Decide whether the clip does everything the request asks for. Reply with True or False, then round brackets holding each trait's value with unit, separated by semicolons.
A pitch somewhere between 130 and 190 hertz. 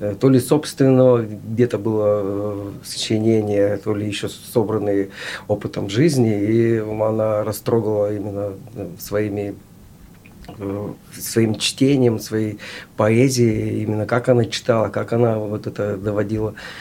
False (110 Hz)